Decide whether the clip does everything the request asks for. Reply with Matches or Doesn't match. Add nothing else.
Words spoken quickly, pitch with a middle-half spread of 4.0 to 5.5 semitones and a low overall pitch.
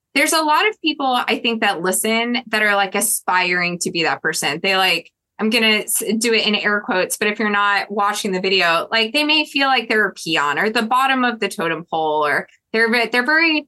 Doesn't match